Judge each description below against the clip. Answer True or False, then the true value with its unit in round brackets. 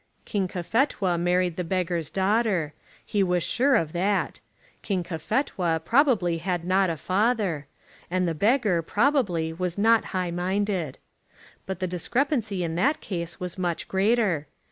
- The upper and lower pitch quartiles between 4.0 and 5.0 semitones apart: False (3.5 semitones)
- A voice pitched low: False (185 Hz)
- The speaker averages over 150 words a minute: False (145 wpm)